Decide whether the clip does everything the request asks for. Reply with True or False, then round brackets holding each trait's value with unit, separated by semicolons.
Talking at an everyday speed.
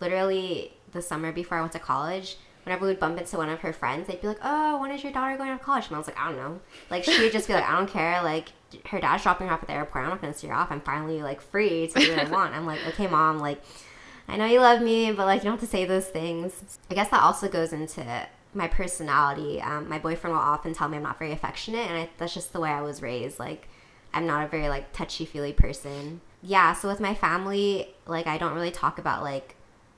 False (270 wpm)